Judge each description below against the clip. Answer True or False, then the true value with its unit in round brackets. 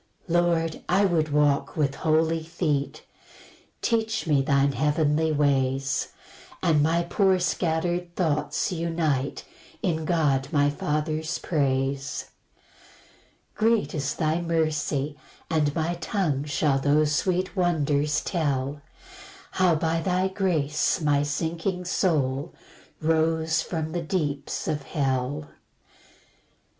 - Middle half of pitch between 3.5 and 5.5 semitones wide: False (2.9 semitones)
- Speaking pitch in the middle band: True (155 Hz)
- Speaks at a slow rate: True (110 wpm)